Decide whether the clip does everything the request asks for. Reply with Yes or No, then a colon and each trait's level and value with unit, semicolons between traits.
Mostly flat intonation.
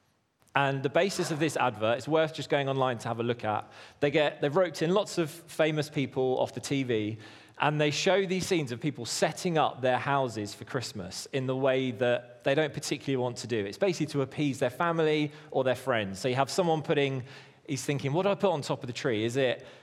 No: average, 3.8 semitones